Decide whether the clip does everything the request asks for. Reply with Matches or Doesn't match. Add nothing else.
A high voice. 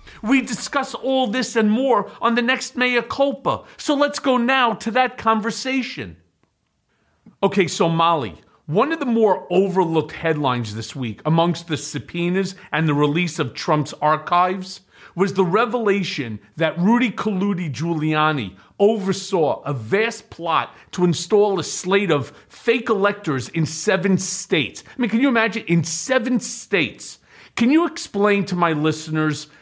Matches